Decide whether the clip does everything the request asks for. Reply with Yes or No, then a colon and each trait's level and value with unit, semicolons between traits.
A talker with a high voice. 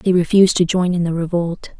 No: medium, 175 Hz